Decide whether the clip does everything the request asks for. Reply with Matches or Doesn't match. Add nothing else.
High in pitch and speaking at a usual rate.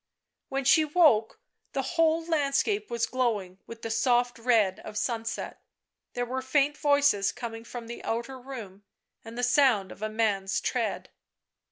Matches